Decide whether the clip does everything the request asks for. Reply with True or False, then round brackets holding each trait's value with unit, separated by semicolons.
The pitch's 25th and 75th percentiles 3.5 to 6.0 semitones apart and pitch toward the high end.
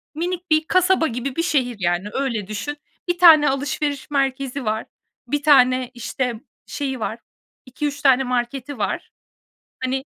False (3.0 semitones; 270 Hz)